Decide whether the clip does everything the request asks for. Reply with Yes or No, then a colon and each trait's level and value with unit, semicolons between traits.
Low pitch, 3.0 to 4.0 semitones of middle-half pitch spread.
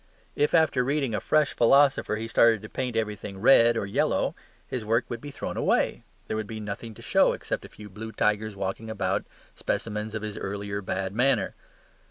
No: low, 110 Hz; narrow, 2.6 semitones